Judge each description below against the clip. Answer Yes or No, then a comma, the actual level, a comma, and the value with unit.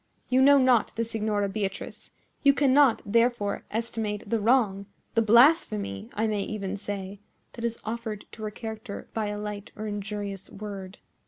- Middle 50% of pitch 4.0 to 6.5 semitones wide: No, narrow, 2.4 semitones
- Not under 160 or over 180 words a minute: No, average, 150 wpm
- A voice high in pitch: Yes, high, 215 Hz